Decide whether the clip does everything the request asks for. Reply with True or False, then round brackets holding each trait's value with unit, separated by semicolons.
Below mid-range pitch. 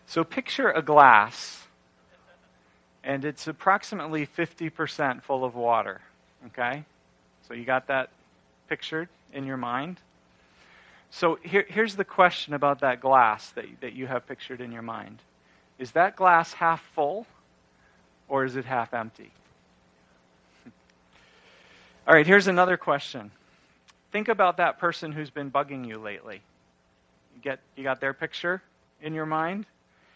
True (130 Hz)